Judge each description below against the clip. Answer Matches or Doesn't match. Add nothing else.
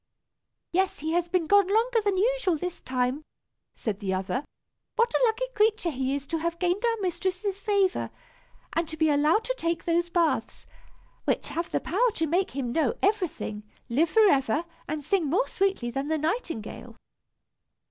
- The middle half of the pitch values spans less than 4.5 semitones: Doesn't match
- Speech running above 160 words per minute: Matches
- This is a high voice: Matches